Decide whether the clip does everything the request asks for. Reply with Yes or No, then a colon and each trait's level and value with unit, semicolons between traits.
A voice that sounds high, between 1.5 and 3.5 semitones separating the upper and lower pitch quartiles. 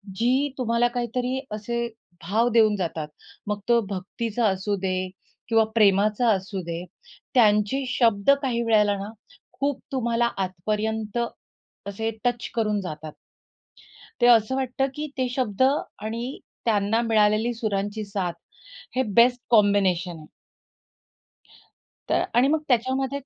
Yes: high, 220 Hz; average, 3.1 semitones